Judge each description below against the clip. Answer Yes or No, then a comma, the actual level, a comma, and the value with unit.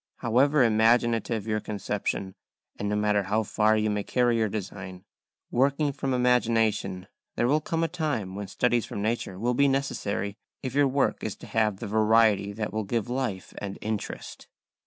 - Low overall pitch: Yes, low, 110 Hz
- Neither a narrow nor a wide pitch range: Yes, average, 3.2 semitones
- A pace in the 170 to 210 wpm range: Yes, average, 175 wpm